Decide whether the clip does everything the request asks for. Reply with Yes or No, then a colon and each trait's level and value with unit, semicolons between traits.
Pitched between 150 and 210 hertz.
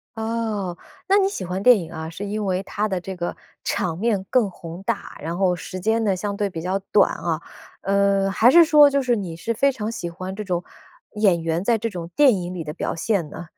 Yes: high, 195 Hz